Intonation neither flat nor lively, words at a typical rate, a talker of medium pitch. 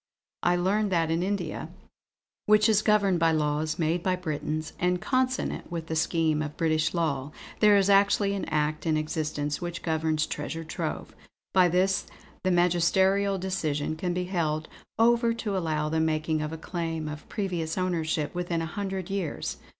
Yes: average, 3.5 semitones; average, 165 wpm; medium, 170 Hz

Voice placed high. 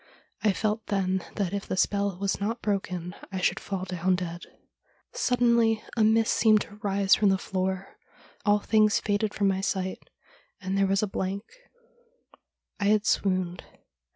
Yes: high, 200 Hz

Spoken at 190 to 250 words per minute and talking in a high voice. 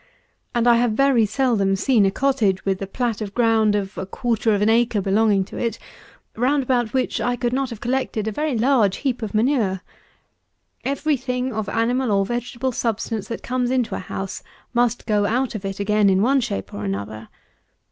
Yes: average, 200 wpm; high, 230 Hz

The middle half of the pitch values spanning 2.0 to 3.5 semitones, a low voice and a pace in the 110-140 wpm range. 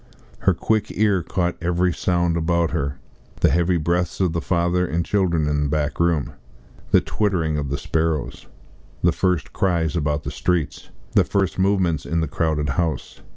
No: average, 2.8 semitones; very low, 85 Hz; average, 170 wpm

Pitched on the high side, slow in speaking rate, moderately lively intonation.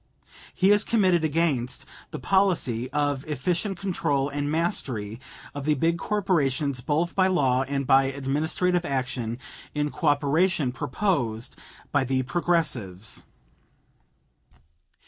No: medium, 145 Hz; slow, 110 wpm; average, 4.7 semitones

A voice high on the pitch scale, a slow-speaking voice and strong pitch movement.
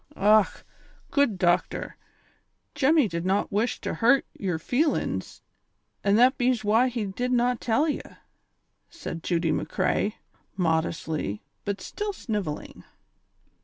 Yes: high, 215 Hz; slow, 120 wpm; wide, 5.7 semitones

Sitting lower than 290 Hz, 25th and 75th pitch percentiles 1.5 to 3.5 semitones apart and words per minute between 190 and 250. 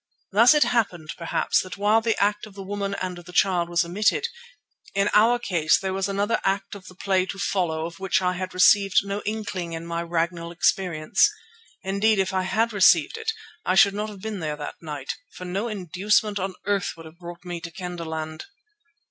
Yes: high, 190 Hz; average, 3.0 semitones; average, 200 wpm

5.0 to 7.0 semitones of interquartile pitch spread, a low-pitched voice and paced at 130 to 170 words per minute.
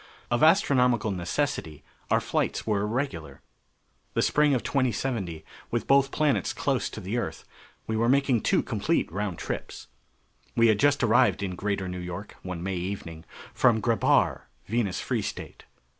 Yes: wide, 5.6 semitones; low, 110 Hz; average, 155 wpm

